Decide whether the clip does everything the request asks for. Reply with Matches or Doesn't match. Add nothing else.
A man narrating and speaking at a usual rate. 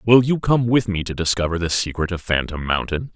Doesn't match